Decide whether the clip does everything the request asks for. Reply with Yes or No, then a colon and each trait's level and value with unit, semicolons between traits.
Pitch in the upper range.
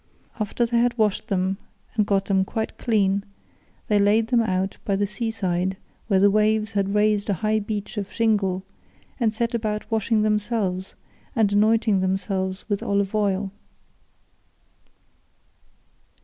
Yes: high, 210 Hz